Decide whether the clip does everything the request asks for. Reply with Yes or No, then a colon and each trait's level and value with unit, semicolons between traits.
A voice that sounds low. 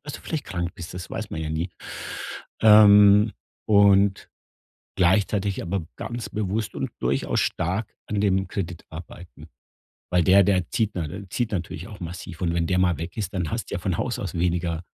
Yes: very low, 95 Hz